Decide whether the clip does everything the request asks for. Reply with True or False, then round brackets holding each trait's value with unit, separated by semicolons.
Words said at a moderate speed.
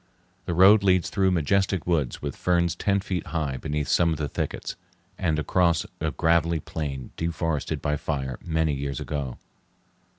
True (160 wpm)